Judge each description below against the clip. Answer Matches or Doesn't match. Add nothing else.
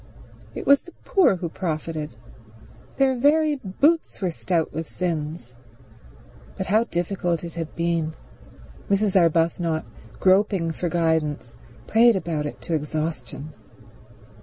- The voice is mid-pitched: Matches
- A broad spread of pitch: Doesn't match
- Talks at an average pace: Doesn't match